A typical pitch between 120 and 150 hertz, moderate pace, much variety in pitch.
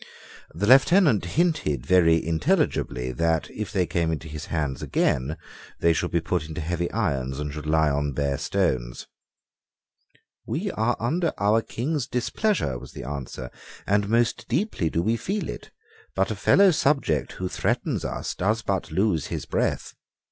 No: very low, 85 Hz; average, 160 wpm; wide, 7.7 semitones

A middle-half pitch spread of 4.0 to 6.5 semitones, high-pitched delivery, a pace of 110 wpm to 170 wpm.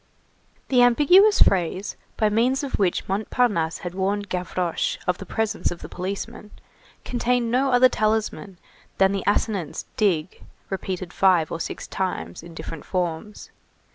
Yes: average, 4.4 semitones; high, 200 Hz; average, 140 wpm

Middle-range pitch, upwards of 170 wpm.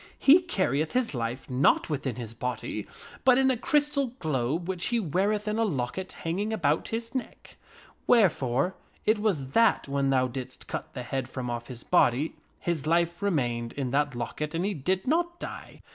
Yes: medium, 160 Hz; average, 185 wpm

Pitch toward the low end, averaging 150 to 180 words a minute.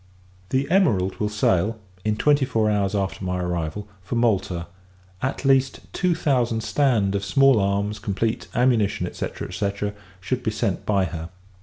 Yes: low, 105 Hz; average, 155 wpm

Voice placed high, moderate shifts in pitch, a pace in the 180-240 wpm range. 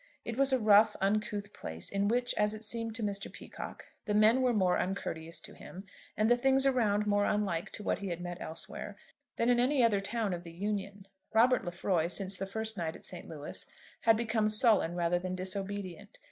Yes: high, 205 Hz; average, 3.4 semitones; fast, 205 wpm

